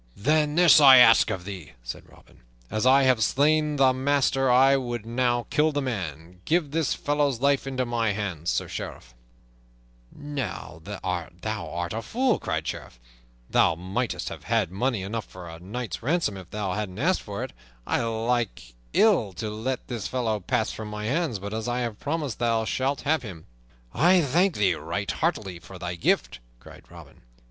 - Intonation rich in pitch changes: Yes, wide, 5.8 semitones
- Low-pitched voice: Yes, low, 120 Hz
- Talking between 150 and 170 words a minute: No, average, 180 wpm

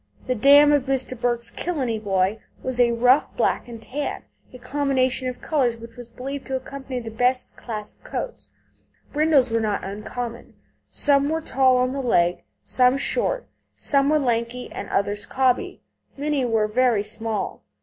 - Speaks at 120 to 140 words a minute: No, average, 165 wpm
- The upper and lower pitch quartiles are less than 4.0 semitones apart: Yes, average, 3.1 semitones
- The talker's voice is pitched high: Yes, very high, 250 Hz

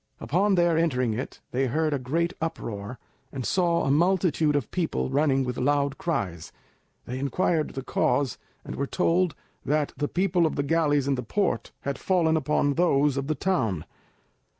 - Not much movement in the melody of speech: No, average, 4.1 semitones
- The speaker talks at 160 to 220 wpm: Yes, average, 175 wpm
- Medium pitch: Yes, medium, 145 Hz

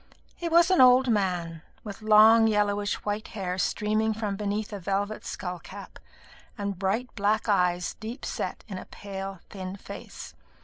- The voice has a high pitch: Yes, high, 205 Hz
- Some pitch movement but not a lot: No, narrow, 2.1 semitones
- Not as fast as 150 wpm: No, average, 160 wpm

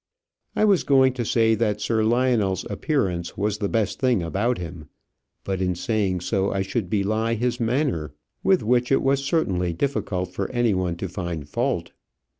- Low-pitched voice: Yes, low, 105 Hz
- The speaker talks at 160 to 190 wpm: Yes, average, 175 wpm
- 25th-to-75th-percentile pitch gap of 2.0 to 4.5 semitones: No, average, 5.1 semitones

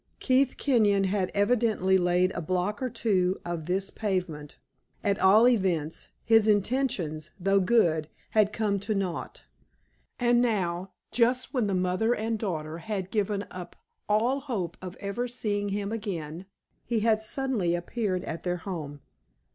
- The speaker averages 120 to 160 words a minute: Yes, average, 145 wpm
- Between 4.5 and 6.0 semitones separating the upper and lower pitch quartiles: No, average, 3.8 semitones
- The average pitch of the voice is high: Yes, high, 200 Hz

